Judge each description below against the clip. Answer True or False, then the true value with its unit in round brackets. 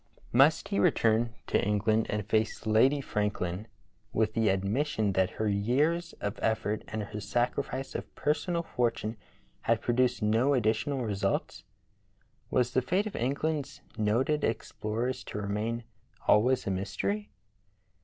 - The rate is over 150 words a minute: False (135 wpm)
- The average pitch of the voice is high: False (115 Hz)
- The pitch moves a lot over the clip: False (4.1 semitones)